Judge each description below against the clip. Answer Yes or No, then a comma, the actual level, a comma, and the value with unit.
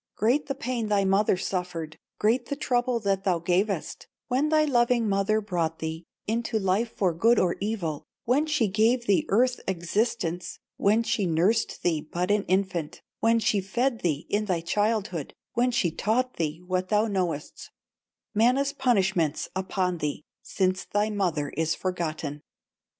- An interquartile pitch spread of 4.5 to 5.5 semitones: Yes, average, 4.8 semitones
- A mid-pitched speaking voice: No, high, 200 Hz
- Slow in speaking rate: No, average, 155 wpm